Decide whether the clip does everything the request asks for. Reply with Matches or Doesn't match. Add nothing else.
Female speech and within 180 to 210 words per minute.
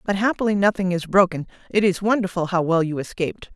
Matches